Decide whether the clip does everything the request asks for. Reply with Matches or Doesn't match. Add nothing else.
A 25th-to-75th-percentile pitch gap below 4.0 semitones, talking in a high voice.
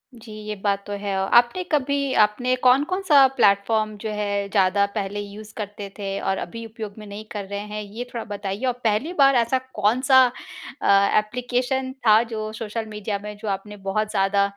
Matches